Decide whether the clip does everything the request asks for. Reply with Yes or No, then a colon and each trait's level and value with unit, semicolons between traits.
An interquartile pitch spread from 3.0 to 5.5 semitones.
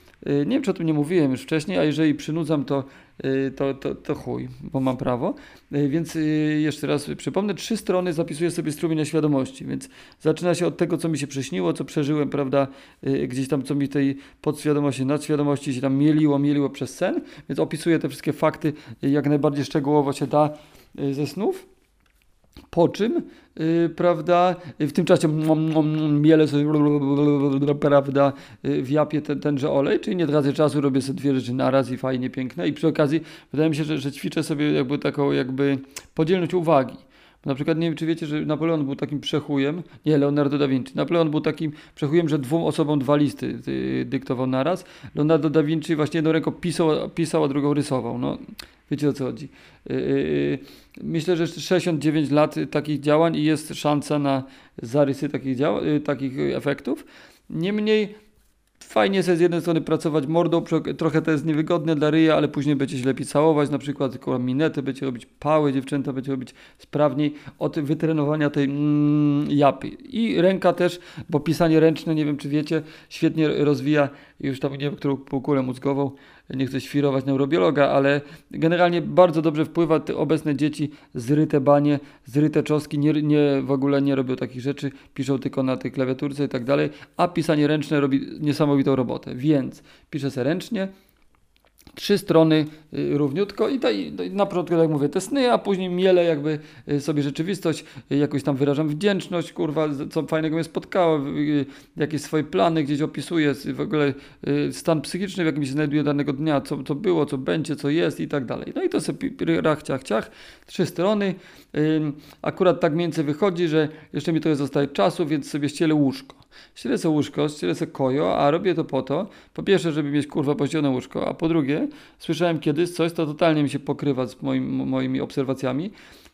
No: narrow, 2.4 semitones